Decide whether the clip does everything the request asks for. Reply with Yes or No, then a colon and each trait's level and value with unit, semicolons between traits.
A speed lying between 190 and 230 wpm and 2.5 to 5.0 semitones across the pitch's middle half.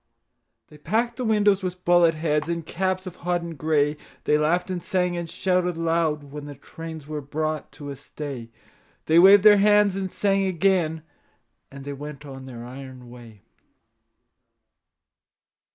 No: average, 155 wpm; average, 4.1 semitones